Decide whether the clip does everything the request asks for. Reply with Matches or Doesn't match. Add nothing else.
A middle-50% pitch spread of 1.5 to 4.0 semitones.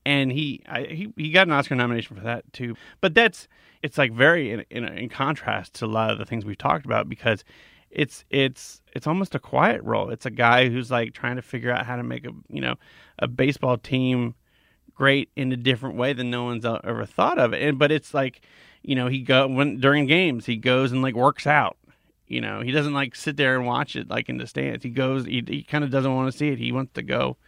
Matches